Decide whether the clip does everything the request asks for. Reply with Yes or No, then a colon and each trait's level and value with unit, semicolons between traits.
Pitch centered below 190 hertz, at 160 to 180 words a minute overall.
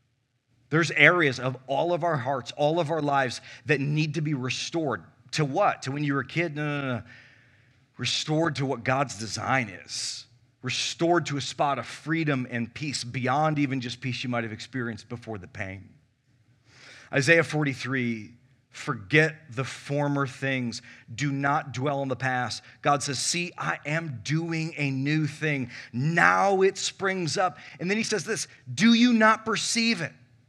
Yes: low, 135 Hz; average, 170 wpm